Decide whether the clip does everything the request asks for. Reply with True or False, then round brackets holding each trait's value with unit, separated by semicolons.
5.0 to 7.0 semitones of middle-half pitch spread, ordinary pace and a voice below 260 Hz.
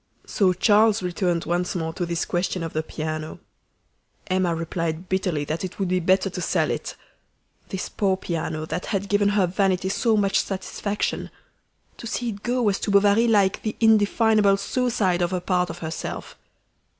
False (2.8 semitones; 175 wpm; 190 Hz)